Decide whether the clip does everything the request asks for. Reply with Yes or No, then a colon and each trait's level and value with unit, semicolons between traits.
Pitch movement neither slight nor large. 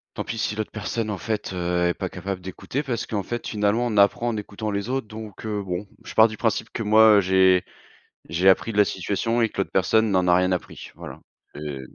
Yes: average, 3.0 semitones